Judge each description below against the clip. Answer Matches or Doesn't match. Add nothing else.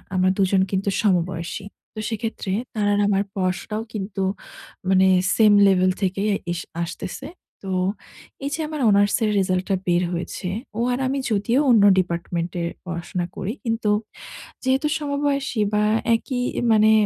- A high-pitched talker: Matches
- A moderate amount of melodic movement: Matches